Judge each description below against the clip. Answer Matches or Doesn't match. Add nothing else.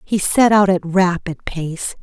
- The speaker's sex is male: Doesn't match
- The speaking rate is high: Doesn't match